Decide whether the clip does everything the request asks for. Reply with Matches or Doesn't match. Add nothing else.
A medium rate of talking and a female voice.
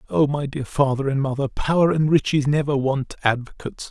Doesn't match